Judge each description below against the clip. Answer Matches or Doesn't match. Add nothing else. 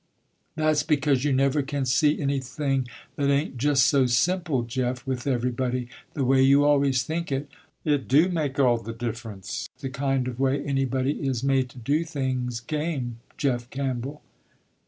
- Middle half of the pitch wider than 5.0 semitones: Doesn't match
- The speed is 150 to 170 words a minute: Matches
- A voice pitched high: Doesn't match